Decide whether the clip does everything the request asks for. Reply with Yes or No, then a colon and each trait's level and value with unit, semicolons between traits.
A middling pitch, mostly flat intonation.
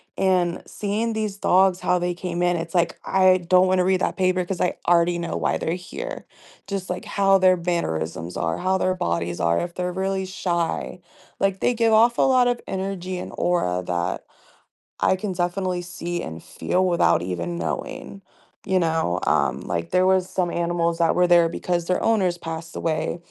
Yes: medium, 180 Hz; narrow, 2.0 semitones